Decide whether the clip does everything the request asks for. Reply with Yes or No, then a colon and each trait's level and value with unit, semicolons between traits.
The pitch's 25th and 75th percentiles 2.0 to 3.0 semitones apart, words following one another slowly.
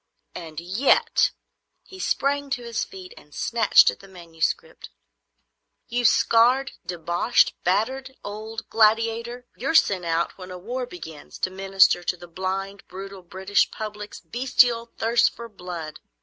No: average, 4.8 semitones; slow, 130 wpm